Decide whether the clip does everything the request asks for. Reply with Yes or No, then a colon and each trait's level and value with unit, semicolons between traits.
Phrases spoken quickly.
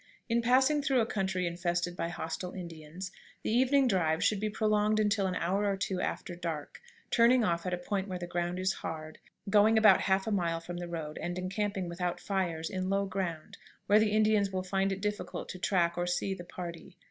Yes: fast, 210 wpm